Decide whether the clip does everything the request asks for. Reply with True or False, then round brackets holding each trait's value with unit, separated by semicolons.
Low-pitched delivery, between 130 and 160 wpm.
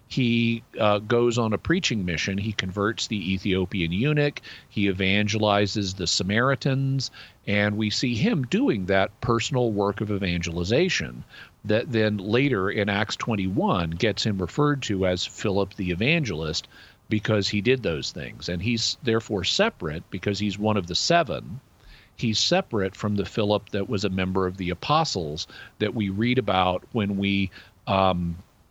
True (105 Hz; 155 wpm)